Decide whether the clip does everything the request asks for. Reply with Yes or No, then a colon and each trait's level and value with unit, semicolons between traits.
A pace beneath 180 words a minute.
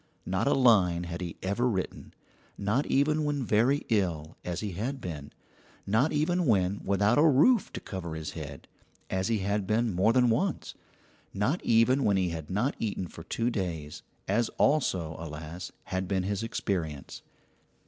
Yes: average, 170 wpm